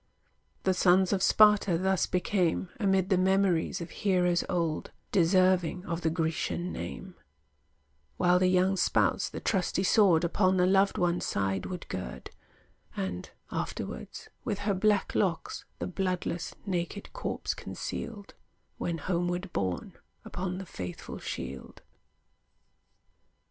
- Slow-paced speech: Yes, slow, 125 wpm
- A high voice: No, medium, 180 Hz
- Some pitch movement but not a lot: No, narrow, 2.1 semitones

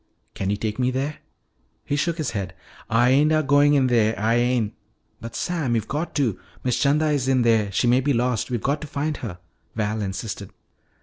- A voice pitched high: No, low, 125 Hz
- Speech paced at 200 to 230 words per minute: Yes, fast, 205 wpm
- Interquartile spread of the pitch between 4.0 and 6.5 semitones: Yes, average, 4.6 semitones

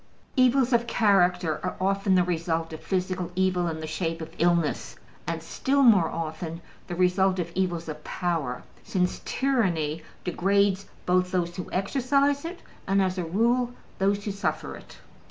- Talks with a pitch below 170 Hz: No, medium, 185 Hz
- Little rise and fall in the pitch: No, average, 3.1 semitones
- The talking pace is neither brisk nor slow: Yes, average, 160 wpm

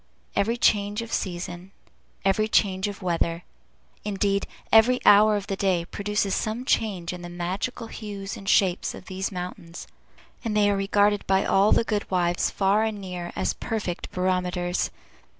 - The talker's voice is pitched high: Yes, high, 195 Hz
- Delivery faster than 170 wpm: No, average, 160 wpm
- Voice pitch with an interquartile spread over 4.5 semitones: No, narrow, 2.5 semitones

